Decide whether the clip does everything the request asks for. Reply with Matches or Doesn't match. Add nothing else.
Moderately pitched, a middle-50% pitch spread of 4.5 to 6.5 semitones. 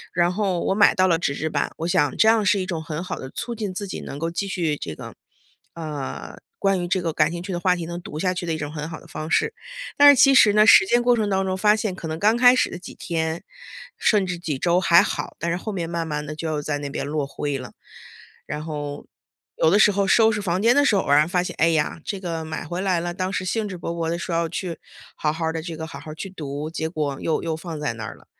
Doesn't match